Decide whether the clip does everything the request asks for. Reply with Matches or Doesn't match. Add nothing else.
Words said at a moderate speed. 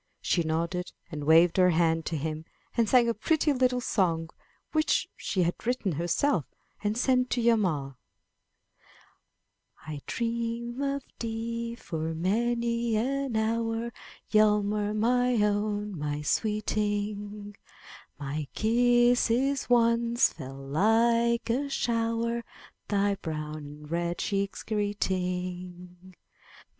Doesn't match